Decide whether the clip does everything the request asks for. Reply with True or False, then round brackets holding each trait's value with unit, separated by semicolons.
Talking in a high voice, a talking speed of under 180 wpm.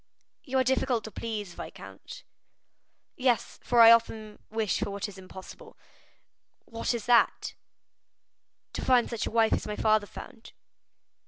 True (225 Hz; 145 wpm)